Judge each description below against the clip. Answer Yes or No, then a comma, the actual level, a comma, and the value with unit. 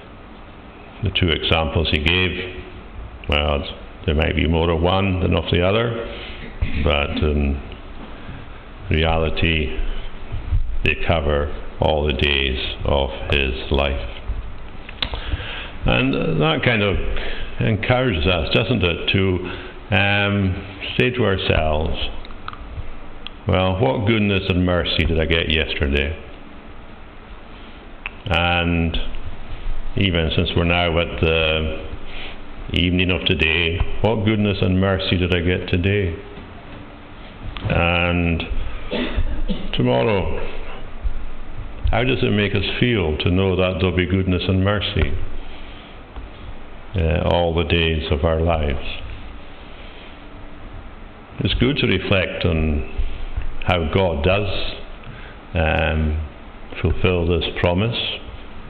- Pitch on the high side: No, very low, 90 Hz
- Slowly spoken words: Yes, slow, 105 wpm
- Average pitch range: Yes, average, 3.2 semitones